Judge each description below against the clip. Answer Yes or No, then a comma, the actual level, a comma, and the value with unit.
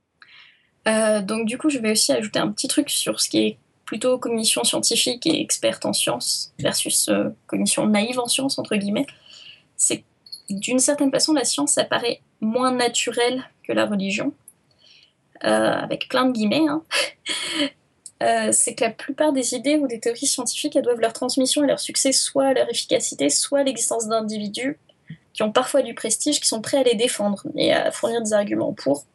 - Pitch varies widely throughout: No, average, 4.5 semitones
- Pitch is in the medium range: No, very high, 250 Hz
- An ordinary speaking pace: Yes, average, 185 wpm